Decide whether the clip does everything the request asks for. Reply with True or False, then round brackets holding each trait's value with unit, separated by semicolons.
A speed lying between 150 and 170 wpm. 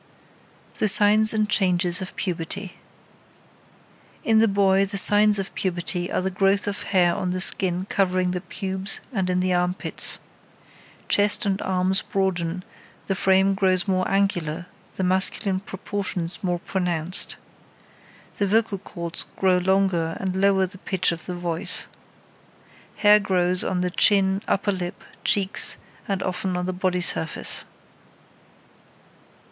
False (135 wpm)